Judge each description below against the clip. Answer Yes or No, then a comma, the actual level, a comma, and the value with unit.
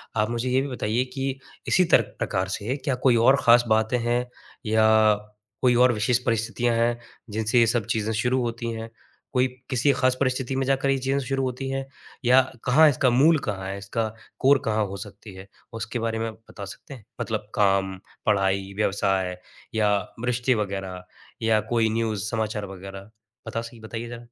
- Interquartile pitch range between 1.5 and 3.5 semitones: Yes, average, 3.2 semitones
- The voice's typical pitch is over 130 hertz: No, low, 115 Hz